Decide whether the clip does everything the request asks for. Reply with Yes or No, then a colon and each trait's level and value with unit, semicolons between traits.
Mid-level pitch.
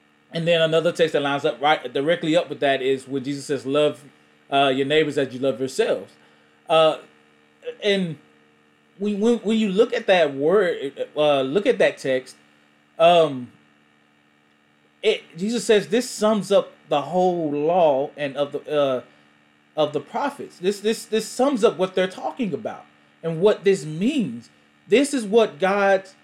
Yes: medium, 155 Hz